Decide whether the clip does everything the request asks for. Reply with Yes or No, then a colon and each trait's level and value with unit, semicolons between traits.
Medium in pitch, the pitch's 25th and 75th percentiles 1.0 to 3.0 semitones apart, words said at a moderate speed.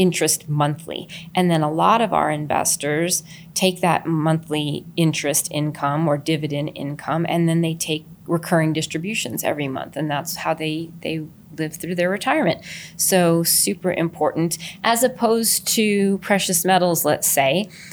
Yes: medium, 165 Hz; narrow, 2.6 semitones; average, 145 wpm